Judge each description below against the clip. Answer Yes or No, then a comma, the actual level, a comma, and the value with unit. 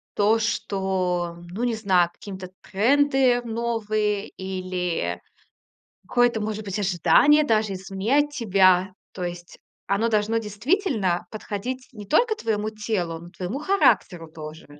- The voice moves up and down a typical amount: Yes, average, 3.8 semitones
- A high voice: Yes, high, 210 Hz